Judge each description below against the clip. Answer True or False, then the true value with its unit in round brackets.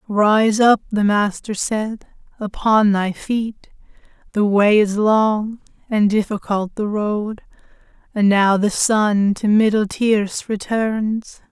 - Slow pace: True (125 wpm)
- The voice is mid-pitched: False (210 Hz)